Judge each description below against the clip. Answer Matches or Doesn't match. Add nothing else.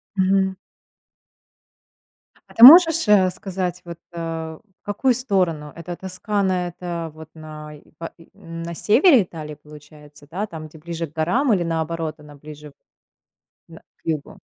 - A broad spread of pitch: Doesn't match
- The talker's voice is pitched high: Doesn't match